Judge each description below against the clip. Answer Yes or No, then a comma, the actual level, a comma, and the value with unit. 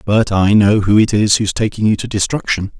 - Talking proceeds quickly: Yes, fast, 235 wpm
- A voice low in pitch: Yes, low, 105 Hz